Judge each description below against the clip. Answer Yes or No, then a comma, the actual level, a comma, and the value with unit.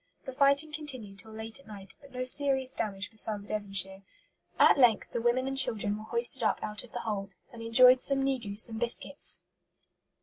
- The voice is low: No, high, 230 Hz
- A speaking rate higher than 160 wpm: Yes, average, 195 wpm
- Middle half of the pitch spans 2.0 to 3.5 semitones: No, average, 3.9 semitones